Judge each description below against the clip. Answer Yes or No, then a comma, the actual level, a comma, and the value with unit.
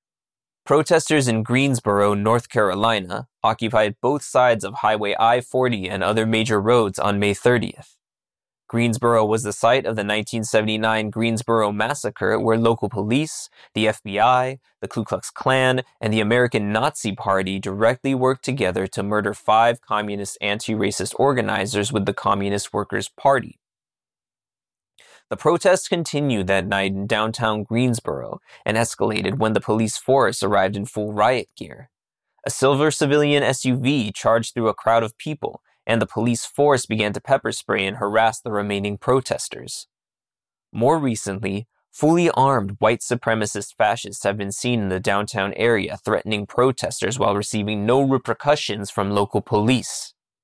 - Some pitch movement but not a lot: Yes, average, 3.5 semitones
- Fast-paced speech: No, average, 145 wpm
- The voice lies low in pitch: Yes, low, 110 Hz